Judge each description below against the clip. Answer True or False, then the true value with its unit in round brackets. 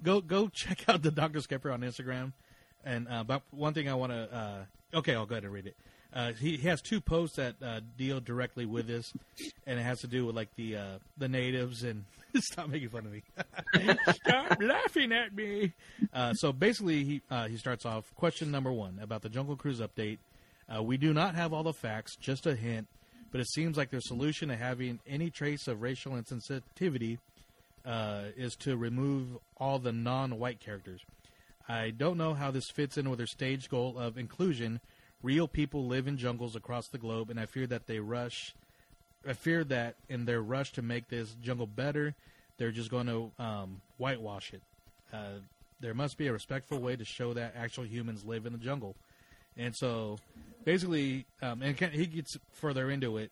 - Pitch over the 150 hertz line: False (125 Hz)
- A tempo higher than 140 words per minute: True (200 wpm)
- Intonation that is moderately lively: True (3.9 semitones)